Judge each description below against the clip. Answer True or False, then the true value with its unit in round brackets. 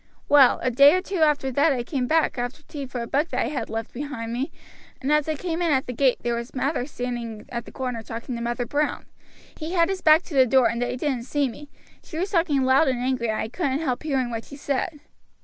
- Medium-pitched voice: False (265 Hz)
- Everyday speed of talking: False (255 wpm)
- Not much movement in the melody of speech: False (3.8 semitones)